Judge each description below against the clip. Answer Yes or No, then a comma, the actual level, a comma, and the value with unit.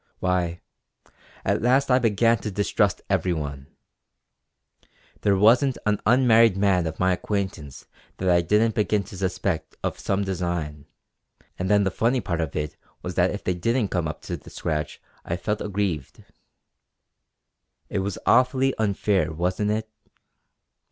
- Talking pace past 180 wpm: No, average, 145 wpm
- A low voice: Yes, very low, 95 Hz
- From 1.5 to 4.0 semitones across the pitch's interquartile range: Yes, average, 3.6 semitones